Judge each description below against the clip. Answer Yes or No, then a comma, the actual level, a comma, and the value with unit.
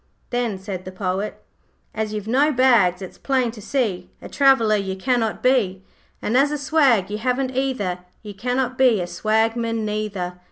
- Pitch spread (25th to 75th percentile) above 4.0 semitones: Yes, average, 4.6 semitones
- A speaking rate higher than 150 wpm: Yes, average, 170 wpm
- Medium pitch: No, high, 220 Hz